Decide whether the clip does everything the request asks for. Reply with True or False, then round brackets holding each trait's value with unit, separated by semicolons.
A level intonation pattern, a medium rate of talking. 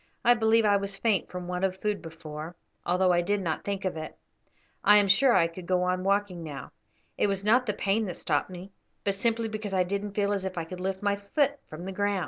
False (2.3 semitones; 245 wpm)